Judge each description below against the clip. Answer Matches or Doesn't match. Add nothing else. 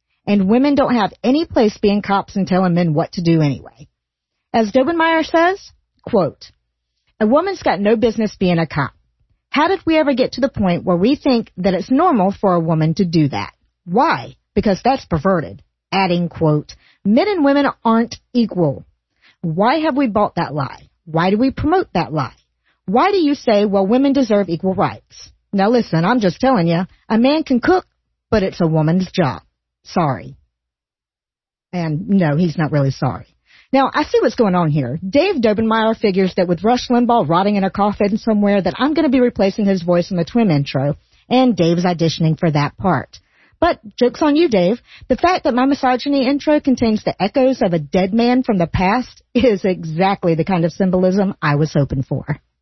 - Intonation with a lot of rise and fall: Matches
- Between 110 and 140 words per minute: Doesn't match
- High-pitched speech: Matches